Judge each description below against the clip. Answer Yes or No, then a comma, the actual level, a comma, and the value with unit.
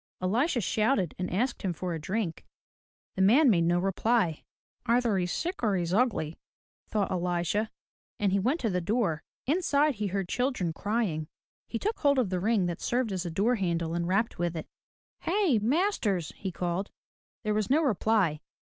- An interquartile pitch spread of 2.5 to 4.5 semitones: No, wide, 5.5 semitones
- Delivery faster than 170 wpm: Yes, average, 180 wpm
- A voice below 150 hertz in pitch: No, high, 200 Hz